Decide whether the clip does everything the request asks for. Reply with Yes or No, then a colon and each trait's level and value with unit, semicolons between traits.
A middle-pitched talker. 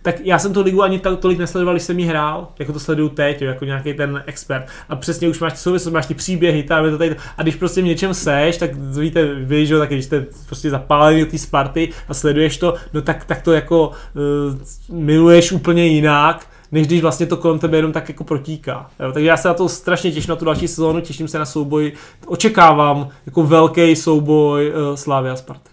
Yes: medium, 160 Hz